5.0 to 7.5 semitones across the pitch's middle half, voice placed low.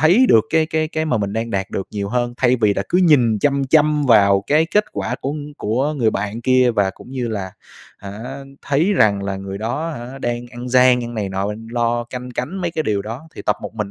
Yes: average, 5.3 semitones; low, 120 Hz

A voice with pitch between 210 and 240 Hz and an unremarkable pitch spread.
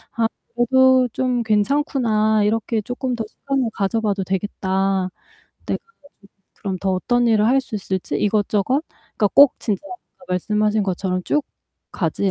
Yes: high, 215 Hz; average, 4.0 semitones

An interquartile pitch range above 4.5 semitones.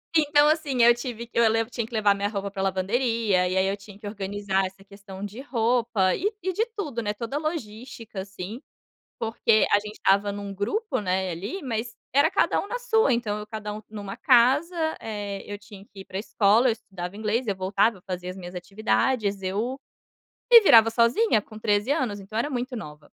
No: average, 3.5 semitones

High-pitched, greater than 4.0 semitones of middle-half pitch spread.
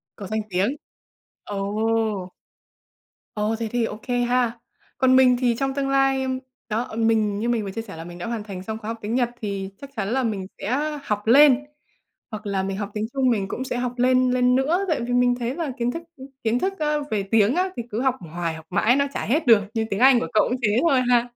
No: high, 235 Hz; average, 3.6 semitones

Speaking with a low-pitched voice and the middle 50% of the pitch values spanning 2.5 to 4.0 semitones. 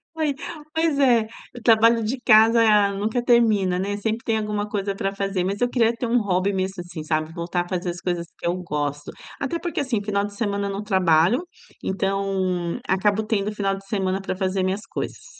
No: high, 200 Hz; average, 3.2 semitones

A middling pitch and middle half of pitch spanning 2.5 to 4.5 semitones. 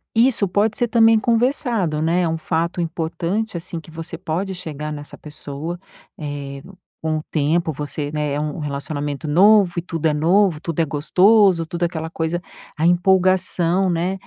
Yes: medium, 165 Hz; average, 3.6 semitones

